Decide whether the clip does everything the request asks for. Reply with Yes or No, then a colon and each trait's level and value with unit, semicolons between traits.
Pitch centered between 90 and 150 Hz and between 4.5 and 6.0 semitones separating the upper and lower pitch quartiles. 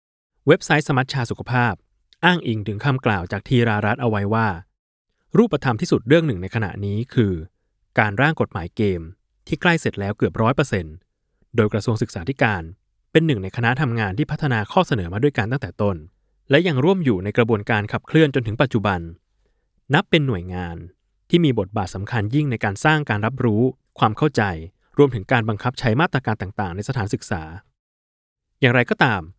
Yes: low, 115 Hz; average, 5.1 semitones